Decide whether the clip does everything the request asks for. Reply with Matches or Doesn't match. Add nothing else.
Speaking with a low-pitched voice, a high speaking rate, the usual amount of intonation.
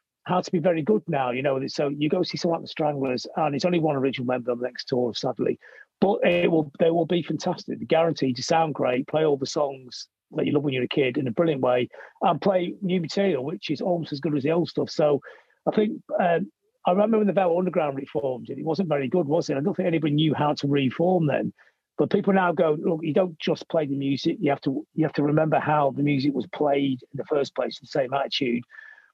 Doesn't match